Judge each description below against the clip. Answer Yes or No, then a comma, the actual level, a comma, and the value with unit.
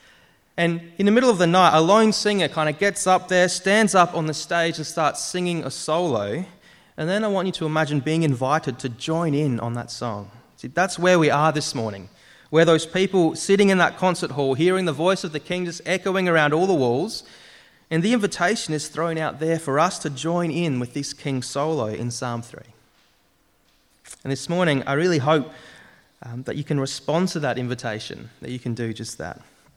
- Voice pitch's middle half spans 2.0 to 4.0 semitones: No, average, 4.7 semitones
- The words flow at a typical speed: No, fast, 215 wpm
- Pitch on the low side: No, medium, 160 Hz